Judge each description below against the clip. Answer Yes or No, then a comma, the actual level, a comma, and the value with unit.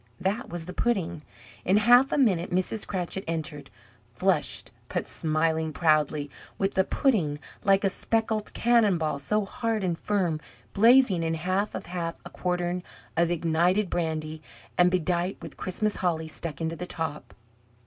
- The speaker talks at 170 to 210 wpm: No, average, 155 wpm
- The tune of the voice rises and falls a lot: No, average, 3.9 semitones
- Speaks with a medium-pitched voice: Yes, medium, 180 Hz